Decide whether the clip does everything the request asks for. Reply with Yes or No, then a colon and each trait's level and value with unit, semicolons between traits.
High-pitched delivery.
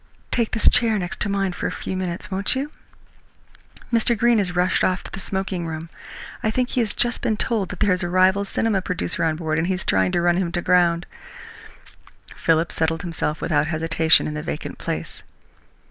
No: medium, 180 Hz